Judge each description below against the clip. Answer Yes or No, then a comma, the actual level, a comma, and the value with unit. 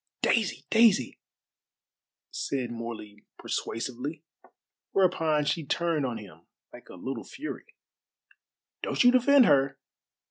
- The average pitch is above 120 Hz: Yes, medium, 140 Hz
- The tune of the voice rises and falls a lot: Yes, wide, 7.6 semitones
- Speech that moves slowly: Yes, slow, 105 wpm